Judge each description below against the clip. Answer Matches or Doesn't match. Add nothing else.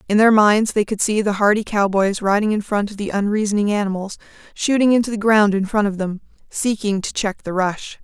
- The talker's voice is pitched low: Doesn't match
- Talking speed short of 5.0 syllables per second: Doesn't match